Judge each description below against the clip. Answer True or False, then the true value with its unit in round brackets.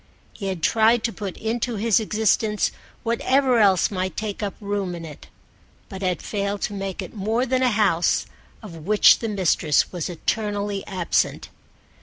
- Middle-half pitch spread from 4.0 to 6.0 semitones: False (2.8 semitones)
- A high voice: True (205 Hz)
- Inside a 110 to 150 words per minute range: False (165 wpm)